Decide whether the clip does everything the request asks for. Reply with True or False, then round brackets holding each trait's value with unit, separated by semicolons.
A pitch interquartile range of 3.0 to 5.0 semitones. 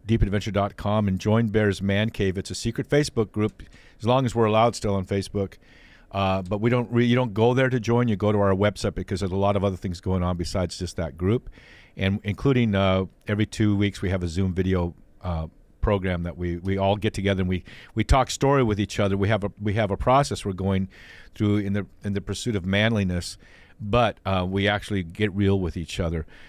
False (2.4 semitones)